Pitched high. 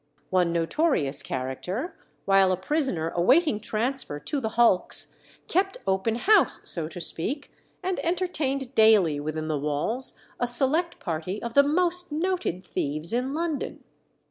Yes: high, 230 Hz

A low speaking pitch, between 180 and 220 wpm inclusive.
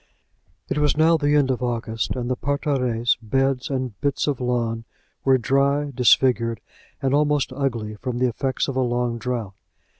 No: low, 130 Hz; average, 170 wpm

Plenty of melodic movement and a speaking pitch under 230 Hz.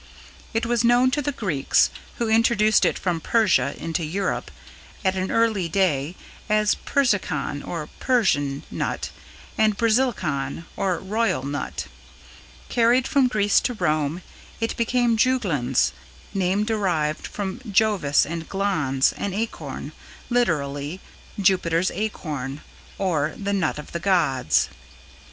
Yes: wide, 6.5 semitones; high, 190 Hz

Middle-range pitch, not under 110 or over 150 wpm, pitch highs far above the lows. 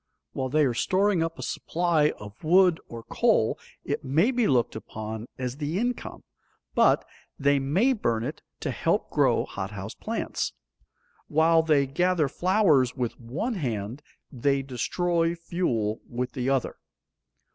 Yes: medium, 145 Hz; average, 145 wpm; wide, 6.0 semitones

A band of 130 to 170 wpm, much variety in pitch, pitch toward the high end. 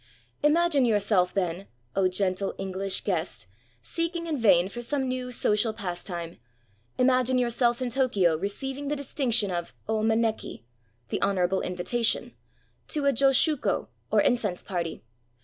Yes: average, 150 wpm; wide, 5.9 semitones; high, 215 Hz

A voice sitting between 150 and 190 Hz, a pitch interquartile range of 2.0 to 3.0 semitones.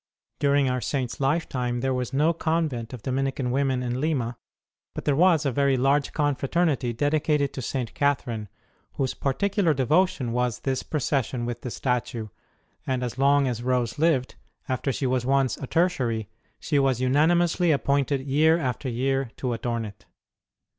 No: low, 135 Hz; average, 2.7 semitones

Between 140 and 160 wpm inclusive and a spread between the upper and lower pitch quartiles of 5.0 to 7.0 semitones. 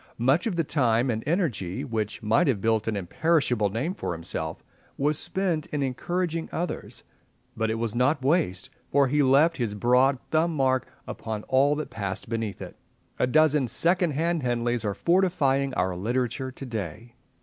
No: average, 170 wpm; wide, 5.6 semitones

